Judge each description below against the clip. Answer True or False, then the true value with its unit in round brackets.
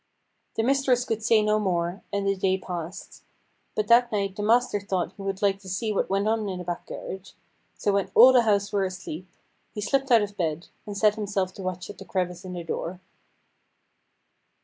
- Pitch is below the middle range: False (200 Hz)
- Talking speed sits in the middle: False (210 wpm)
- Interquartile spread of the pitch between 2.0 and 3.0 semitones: True (2.5 semitones)